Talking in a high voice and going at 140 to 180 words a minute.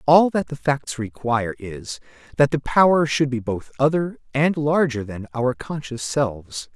No: low, 135 Hz; average, 170 wpm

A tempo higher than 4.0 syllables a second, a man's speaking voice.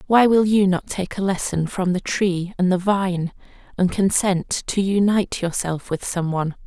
No: 4.6 syllables/s; female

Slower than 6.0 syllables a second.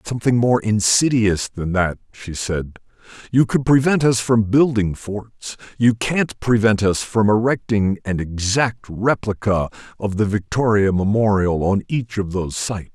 Yes: 4.4 syllables/s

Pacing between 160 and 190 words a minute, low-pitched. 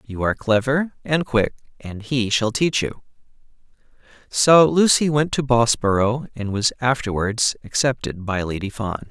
No: average, 145 wpm; low, 120 Hz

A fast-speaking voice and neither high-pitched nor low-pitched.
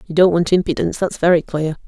Yes: fast, 225 wpm; medium, 170 Hz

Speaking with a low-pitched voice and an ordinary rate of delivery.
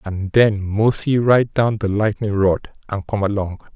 Yes: low, 105 Hz; average, 175 wpm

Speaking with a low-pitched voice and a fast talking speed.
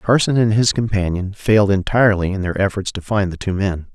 Yes: low, 100 Hz; fast, 215 wpm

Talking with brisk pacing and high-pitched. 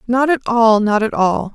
No: average, 195 wpm; high, 225 Hz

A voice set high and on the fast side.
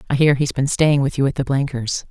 No: medium, 140 Hz; fast, 285 wpm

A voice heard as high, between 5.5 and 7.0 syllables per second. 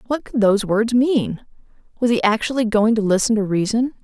Yes: high, 225 Hz; 5.6 syllables/s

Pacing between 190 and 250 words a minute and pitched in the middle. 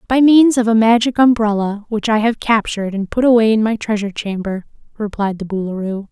No: average, 195 wpm; high, 220 Hz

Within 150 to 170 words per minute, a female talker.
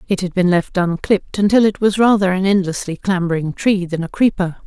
No: fast, 205 wpm; female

